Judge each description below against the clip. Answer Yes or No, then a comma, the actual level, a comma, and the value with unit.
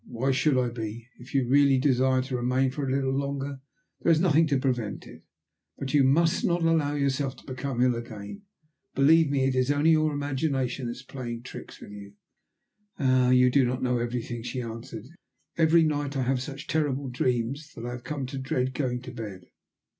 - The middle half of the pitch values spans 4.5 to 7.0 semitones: No, narrow, 2.5 semitones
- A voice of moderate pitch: No, low, 130 Hz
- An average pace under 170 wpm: No, average, 200 wpm